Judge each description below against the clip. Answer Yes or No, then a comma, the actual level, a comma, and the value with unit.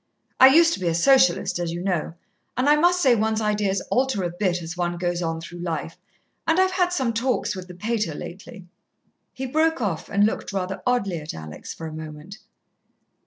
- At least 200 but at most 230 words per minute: Yes, fast, 205 wpm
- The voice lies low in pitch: No, high, 195 Hz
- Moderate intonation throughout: No, wide, 6.7 semitones